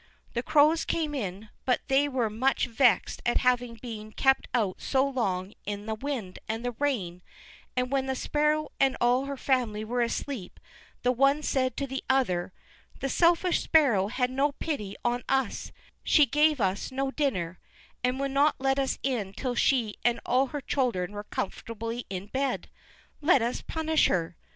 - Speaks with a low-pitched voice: No, very high, 255 Hz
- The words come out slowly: No, average, 175 wpm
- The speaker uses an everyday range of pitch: Yes, average, 4.1 semitones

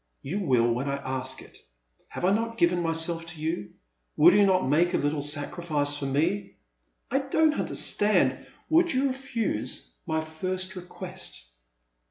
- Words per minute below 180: Yes, average, 165 wpm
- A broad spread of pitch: Yes, wide, 5.8 semitones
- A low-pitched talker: No, medium, 170 Hz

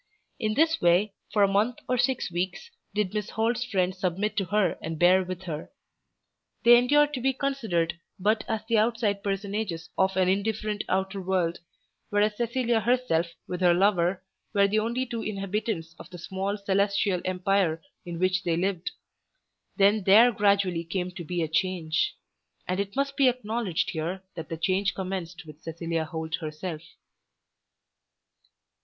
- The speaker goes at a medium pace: Yes, average, 160 wpm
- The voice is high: Yes, high, 195 Hz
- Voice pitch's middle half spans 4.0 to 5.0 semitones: No, average, 3.6 semitones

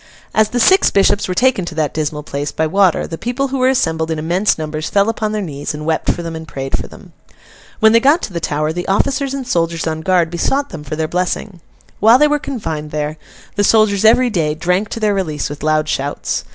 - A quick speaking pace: Yes, fast, 235 wpm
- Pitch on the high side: No, medium, 175 Hz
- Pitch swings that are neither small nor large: No, wide, 5.9 semitones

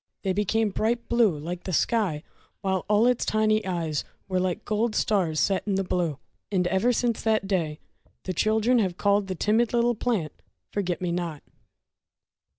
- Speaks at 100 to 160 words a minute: No, average, 170 wpm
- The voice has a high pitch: Yes, high, 200 Hz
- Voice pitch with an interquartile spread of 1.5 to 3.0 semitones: No, average, 3.7 semitones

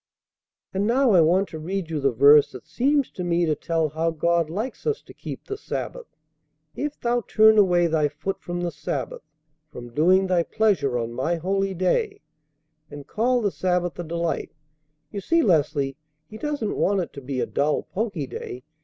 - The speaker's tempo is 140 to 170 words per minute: No, average, 190 wpm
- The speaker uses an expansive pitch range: Yes, wide, 5.8 semitones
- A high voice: No, medium, 175 Hz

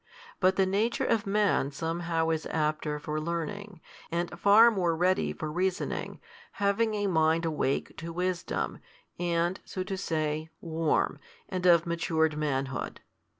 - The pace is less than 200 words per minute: Yes, average, 145 wpm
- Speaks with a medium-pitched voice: Yes, medium, 170 Hz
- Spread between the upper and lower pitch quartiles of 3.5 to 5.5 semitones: No, average, 3.0 semitones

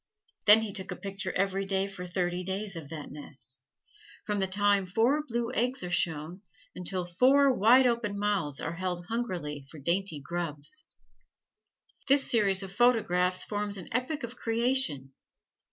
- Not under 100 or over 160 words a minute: Yes, average, 155 wpm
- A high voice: Yes, high, 195 Hz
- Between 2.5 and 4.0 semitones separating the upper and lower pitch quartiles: No, average, 4.5 semitones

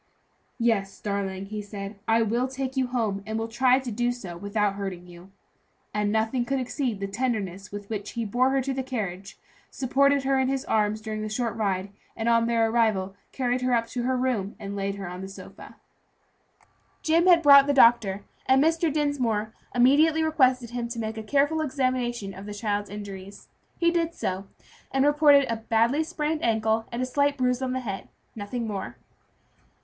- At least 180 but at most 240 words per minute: Yes, average, 195 wpm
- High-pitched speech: Yes, high, 230 Hz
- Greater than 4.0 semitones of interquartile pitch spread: Yes, average, 4.4 semitones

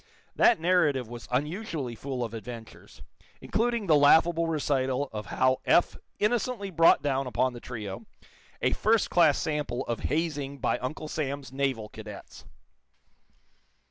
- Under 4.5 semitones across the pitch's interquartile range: No, average, 4.9 semitones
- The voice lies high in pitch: No, medium, 140 Hz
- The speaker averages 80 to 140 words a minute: Yes, slow, 135 wpm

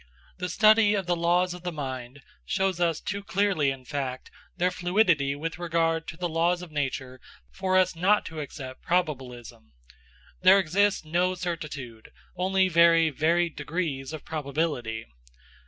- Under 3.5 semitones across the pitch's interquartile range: No, average, 4.3 semitones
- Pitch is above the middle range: No, medium, 165 Hz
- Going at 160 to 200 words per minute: No, average, 150 wpm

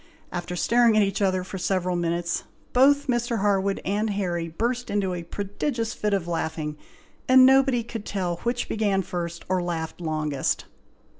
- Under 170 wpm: Yes, average, 160 wpm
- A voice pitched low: No, high, 195 Hz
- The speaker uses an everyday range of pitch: Yes, average, 4.8 semitones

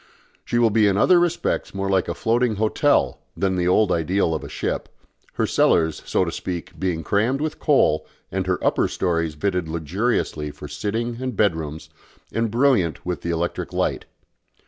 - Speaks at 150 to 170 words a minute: No, average, 180 wpm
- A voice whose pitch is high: No, very low, 95 Hz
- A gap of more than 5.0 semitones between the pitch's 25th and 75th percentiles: Yes, wide, 5.4 semitones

